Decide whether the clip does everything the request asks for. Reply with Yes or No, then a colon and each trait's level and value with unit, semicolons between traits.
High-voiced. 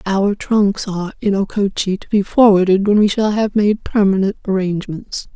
Yes: high, 200 Hz